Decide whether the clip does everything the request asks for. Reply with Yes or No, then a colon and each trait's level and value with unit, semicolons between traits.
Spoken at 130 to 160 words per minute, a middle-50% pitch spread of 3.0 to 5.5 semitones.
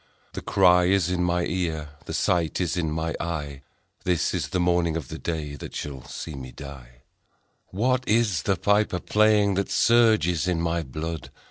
No: average, 175 wpm; average, 3.5 semitones